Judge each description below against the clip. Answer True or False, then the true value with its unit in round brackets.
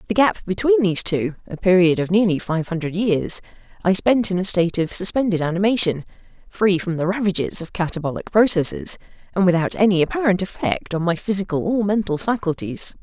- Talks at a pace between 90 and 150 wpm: False (175 wpm)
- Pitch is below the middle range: False (185 Hz)